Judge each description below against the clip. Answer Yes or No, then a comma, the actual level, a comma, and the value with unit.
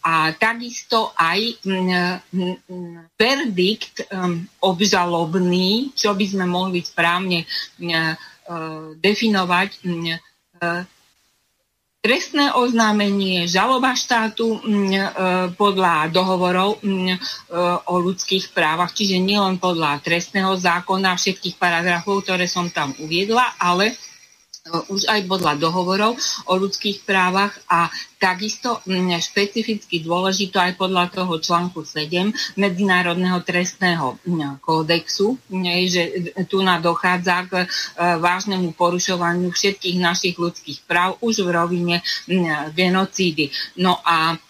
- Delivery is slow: Yes, slow, 105 wpm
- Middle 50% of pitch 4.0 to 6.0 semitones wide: No, narrow, 2.5 semitones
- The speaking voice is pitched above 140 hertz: Yes, medium, 185 Hz